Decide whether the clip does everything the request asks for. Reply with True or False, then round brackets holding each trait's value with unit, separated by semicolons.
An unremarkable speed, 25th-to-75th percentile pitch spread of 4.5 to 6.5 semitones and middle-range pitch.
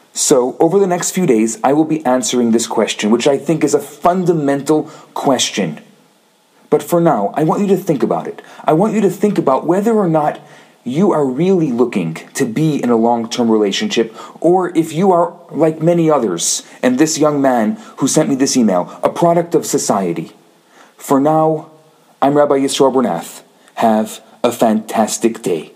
True (180 wpm; 5.1 semitones; 155 Hz)